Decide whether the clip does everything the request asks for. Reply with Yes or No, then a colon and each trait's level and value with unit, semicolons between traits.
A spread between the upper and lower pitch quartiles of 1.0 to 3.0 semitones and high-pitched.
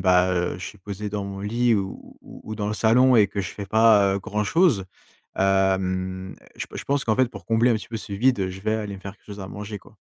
No: narrow, 2.4 semitones; low, 100 Hz